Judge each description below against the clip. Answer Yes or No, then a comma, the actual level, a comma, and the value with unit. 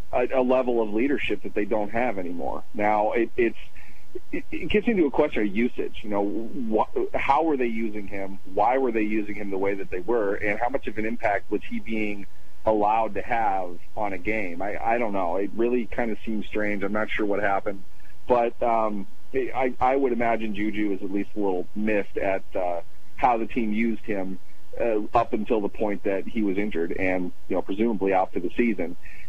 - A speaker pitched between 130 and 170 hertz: No, low, 105 Hz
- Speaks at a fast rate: Yes, fast, 215 wpm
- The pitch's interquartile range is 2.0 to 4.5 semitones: Yes, average, 2.9 semitones